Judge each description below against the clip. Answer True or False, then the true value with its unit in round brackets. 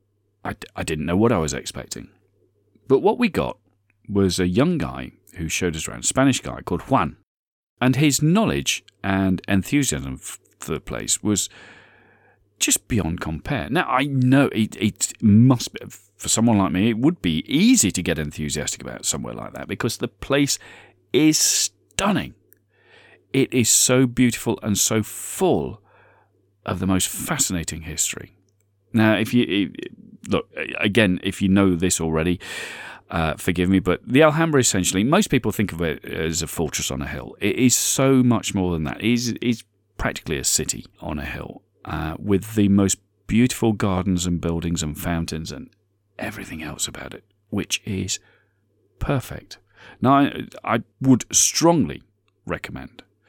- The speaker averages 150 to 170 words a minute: True (160 wpm)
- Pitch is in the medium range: False (100 Hz)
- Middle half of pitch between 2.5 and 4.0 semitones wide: False (4.5 semitones)